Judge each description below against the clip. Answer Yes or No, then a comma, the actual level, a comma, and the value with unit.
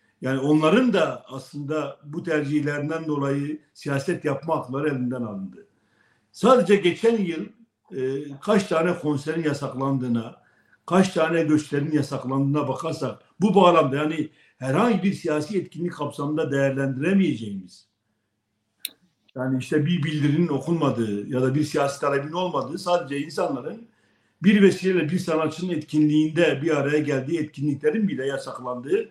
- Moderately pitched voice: Yes, medium, 150 Hz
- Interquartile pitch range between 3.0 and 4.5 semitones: Yes, average, 4.1 semitones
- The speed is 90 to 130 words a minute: Yes, average, 120 wpm